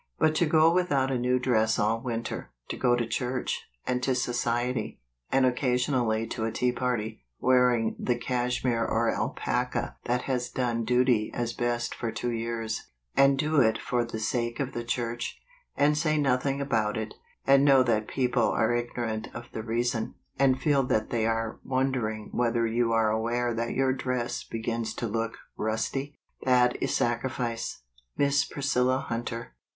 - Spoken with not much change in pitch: Yes, narrow, 2.1 semitones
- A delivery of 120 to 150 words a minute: No, average, 175 wpm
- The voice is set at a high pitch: No, low, 120 Hz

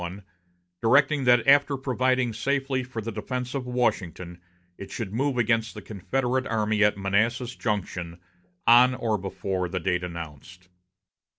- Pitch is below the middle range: Yes, low, 115 Hz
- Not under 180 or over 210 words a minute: No, average, 140 wpm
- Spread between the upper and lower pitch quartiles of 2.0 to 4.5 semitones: No, average, 4.9 semitones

